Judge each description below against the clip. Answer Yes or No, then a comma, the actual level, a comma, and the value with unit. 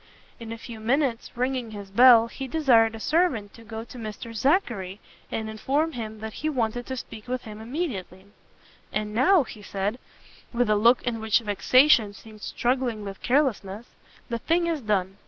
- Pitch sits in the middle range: No, high, 230 Hz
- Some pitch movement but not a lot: Yes, average, 3.3 semitones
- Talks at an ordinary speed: Yes, average, 175 wpm